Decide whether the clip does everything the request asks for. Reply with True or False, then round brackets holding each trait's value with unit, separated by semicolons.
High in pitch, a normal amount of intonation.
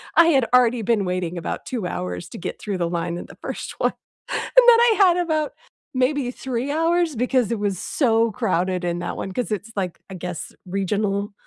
False (220 Hz; 6.5 semitones)